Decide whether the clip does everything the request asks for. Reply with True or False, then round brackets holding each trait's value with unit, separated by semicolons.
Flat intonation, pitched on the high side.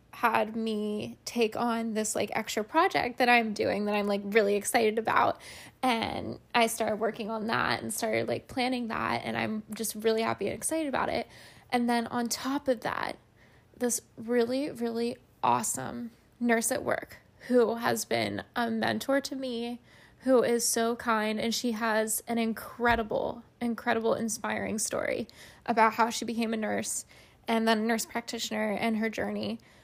True (1.6 semitones; 230 Hz)